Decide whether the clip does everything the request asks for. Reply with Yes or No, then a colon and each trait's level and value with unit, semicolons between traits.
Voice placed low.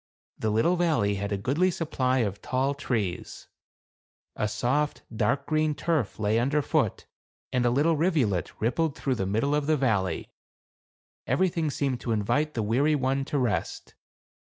Yes: low, 130 Hz